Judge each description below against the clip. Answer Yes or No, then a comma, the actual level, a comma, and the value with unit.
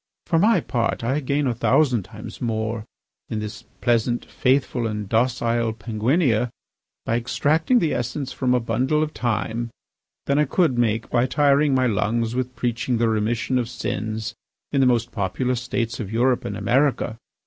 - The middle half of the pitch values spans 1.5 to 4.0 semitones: Yes, average, 2.7 semitones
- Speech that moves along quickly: No, average, 165 wpm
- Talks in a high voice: No, low, 120 Hz